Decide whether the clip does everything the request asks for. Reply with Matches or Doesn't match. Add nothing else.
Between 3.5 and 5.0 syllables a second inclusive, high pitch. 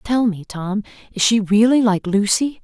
Matches